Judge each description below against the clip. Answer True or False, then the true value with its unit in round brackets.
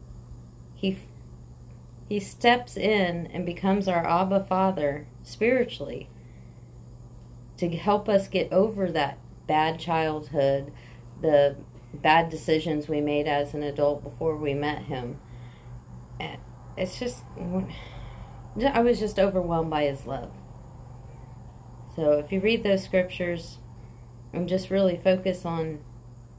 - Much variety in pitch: True (7.2 semitones)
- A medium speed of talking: False (115 wpm)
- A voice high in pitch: False (150 Hz)